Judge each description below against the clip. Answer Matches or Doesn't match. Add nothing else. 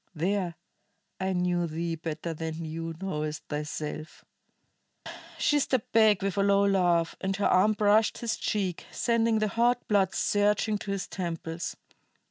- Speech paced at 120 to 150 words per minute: Matches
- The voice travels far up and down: Doesn't match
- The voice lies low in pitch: Doesn't match